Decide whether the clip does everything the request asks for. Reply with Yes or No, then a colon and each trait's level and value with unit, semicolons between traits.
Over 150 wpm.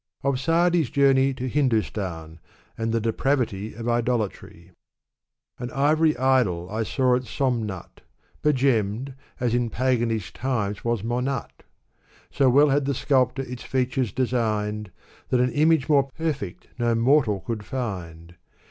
No: slow, 135 wpm